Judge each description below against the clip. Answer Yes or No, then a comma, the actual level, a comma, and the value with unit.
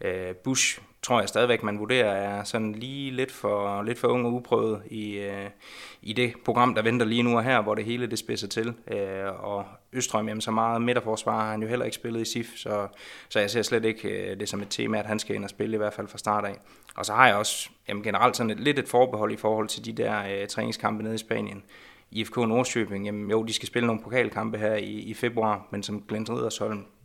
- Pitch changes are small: Yes, narrow, 2.1 semitones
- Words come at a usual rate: No, fast, 240 wpm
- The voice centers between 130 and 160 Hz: No, low, 110 Hz